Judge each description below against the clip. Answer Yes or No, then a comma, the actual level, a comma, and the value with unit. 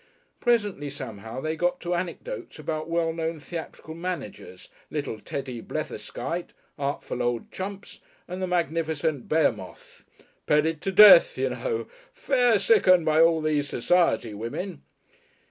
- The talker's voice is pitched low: No, medium, 160 Hz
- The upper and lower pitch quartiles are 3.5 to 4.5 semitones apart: Yes, average, 4.2 semitones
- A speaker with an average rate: No, slow, 130 wpm